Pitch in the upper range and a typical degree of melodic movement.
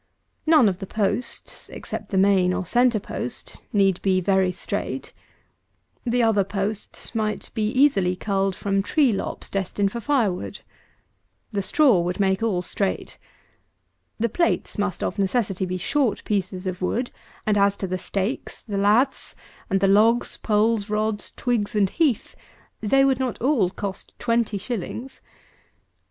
Yes: high, 205 Hz; average, 3.4 semitones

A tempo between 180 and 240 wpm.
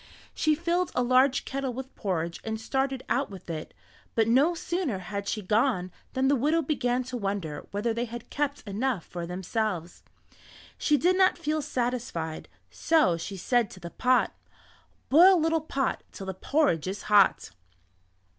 No: average, 165 wpm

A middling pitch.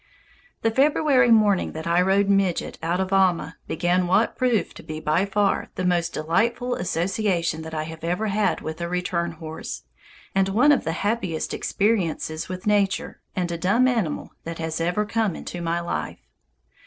Yes: medium, 180 Hz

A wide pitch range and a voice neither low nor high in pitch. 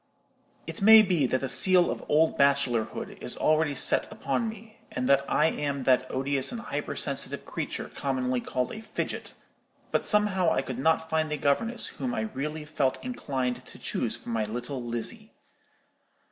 Yes: wide, 6.6 semitones; medium, 145 Hz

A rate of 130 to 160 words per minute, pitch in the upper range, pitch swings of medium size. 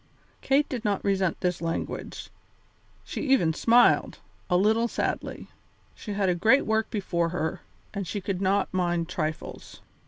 Yes: average, 150 wpm; high, 195 Hz; average, 4.0 semitones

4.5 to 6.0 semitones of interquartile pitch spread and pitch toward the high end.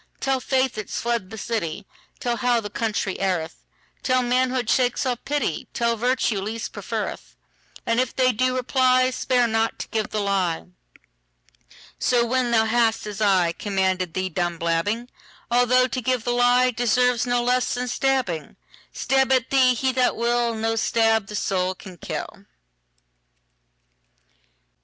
No: average, 4.1 semitones; high, 235 Hz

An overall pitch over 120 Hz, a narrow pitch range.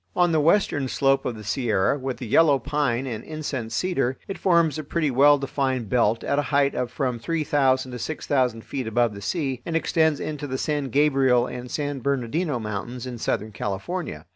No: low, 135 Hz; average, 3.6 semitones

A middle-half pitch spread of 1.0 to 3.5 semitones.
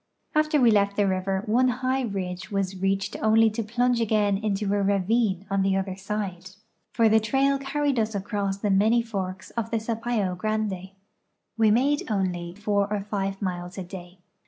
Yes: average, 2.8 semitones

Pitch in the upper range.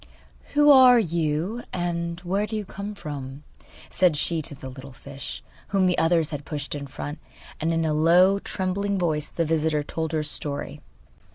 No: medium, 165 Hz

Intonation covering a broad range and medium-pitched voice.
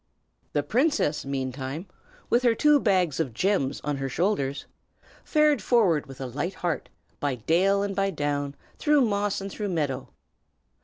Yes: wide, 6.6 semitones; medium, 170 Hz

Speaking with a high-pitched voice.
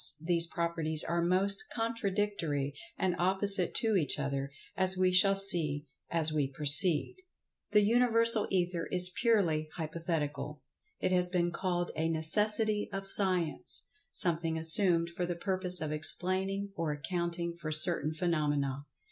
No: medium, 175 Hz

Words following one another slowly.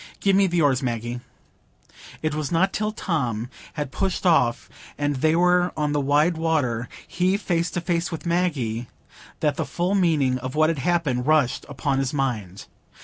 No: average, 165 wpm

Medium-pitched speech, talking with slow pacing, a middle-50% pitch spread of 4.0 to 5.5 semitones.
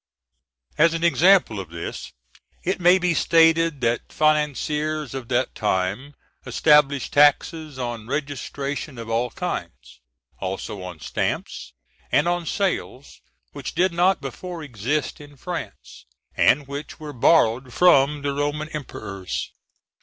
Yes: medium, 145 Hz; slow, 125 wpm; average, 4.9 semitones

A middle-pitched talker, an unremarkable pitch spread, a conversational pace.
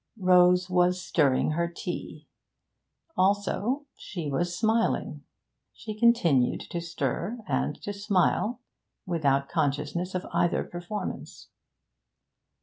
No: medium, 180 Hz; average, 3.5 semitones; slow, 100 wpm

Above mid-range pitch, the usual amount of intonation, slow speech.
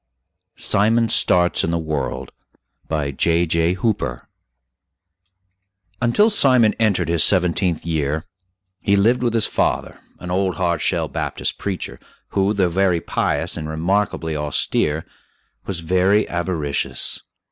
No: very low, 90 Hz; average, 3.8 semitones; slow, 120 wpm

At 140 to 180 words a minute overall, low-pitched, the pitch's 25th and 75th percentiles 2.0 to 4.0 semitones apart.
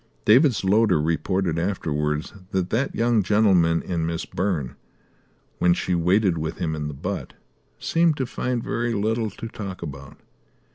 No: average, 150 wpm; very low, 95 Hz; average, 5.1 semitones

